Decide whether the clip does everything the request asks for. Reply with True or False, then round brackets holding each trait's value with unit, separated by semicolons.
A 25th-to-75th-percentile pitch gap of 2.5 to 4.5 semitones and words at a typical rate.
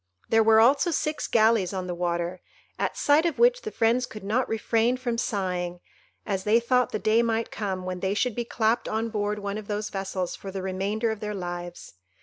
False (3.6 semitones; 210 wpm)